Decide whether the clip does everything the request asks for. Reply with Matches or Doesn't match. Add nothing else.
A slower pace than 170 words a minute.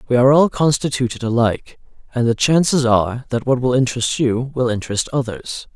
Doesn't match